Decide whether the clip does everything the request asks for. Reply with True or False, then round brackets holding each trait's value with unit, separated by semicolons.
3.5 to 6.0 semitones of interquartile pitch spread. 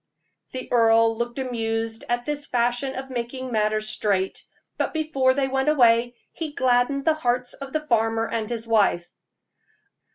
False (2.9 semitones)